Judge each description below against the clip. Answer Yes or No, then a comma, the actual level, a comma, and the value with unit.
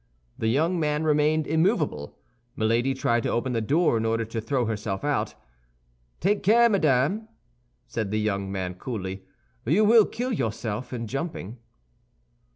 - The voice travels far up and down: Yes, wide, 6.3 semitones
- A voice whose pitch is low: Yes, low, 125 Hz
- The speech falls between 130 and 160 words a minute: Yes, average, 150 wpm